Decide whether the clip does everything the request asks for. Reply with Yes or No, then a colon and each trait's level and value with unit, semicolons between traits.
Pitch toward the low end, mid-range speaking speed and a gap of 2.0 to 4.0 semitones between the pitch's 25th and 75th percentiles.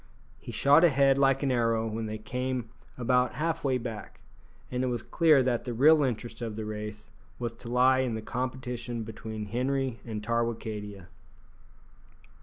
Yes: low, 120 Hz; average, 165 wpm; average, 2.8 semitones